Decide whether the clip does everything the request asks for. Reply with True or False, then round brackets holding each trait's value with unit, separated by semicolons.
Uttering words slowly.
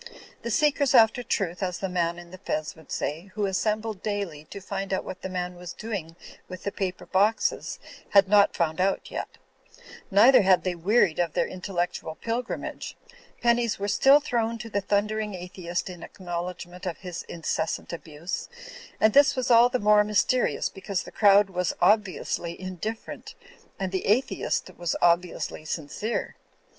False (165 wpm)